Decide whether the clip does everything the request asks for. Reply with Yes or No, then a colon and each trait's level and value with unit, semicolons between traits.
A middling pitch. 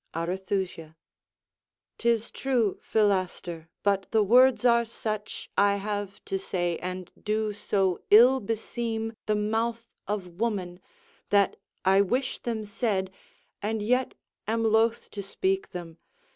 No: high, 210 Hz